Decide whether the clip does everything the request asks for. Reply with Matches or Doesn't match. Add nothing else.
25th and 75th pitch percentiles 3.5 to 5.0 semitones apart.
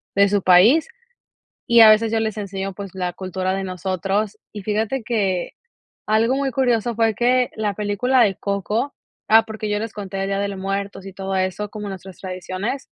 Doesn't match